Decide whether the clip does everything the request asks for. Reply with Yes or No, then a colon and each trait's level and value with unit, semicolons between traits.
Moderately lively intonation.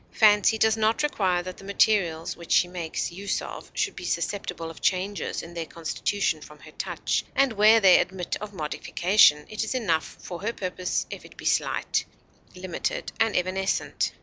Yes: average, 3.6 semitones